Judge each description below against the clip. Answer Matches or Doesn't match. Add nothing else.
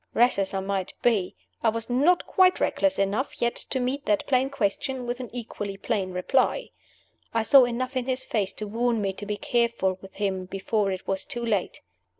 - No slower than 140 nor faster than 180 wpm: Doesn't match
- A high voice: Matches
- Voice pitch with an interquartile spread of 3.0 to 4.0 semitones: Doesn't match